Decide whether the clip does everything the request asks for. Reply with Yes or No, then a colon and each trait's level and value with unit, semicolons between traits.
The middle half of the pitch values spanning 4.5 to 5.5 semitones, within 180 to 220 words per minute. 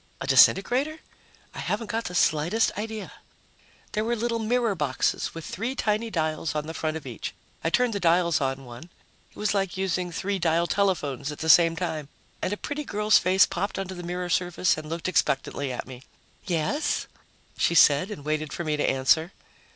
Yes: average, 5.1 semitones; average, 190 wpm